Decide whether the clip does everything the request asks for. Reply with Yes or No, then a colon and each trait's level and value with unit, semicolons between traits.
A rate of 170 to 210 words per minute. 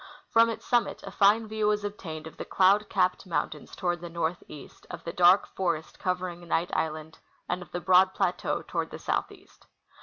Yes: average, 185 wpm